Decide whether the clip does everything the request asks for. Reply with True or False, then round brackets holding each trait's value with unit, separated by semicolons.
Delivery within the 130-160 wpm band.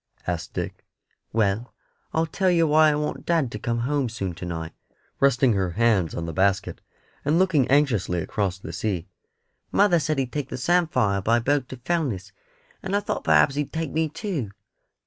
False (190 wpm)